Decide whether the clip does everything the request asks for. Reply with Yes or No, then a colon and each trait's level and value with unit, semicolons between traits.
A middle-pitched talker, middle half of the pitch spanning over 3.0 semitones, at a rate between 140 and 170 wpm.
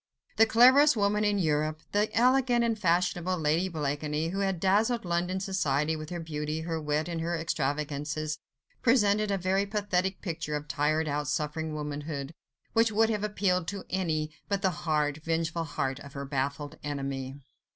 Yes: medium, 165 Hz; average, 4.9 semitones; average, 165 wpm